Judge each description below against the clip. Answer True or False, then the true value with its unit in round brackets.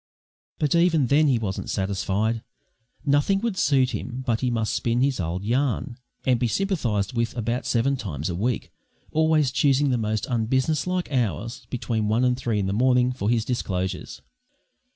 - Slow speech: False (170 wpm)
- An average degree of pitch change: True (4.0 semitones)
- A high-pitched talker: False (125 Hz)